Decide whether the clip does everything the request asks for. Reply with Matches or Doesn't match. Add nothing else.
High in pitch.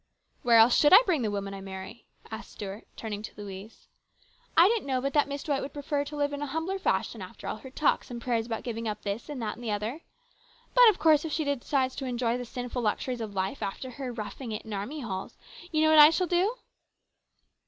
Matches